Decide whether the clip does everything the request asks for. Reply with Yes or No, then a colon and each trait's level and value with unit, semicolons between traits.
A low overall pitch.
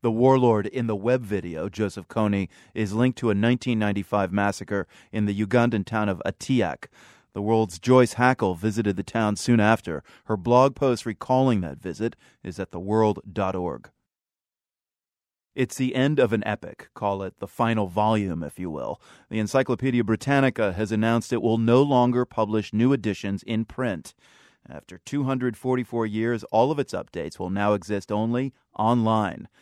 Yes: low, 110 Hz